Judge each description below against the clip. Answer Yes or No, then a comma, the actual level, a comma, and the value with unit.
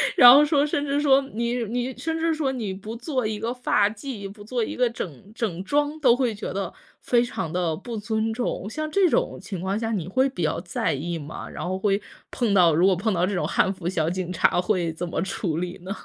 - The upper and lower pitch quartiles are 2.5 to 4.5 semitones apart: No, wide, 5.5 semitones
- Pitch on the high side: Yes, high, 215 Hz